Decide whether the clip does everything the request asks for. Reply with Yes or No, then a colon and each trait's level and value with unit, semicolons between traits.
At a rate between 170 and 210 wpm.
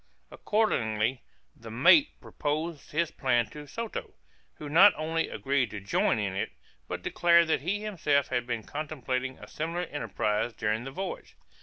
No: average, 155 wpm